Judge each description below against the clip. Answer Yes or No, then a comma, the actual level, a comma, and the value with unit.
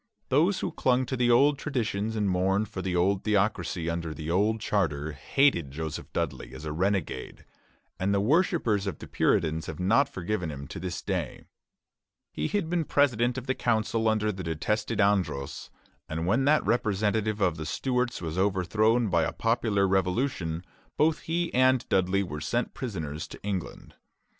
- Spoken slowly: No, average, 170 wpm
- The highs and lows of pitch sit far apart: Yes, wide, 5.9 semitones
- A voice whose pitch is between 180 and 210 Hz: No, low, 100 Hz